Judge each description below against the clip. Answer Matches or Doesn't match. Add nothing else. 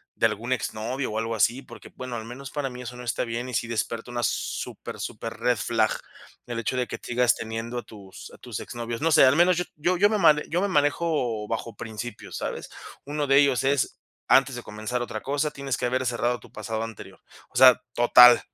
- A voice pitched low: Matches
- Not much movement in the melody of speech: Doesn't match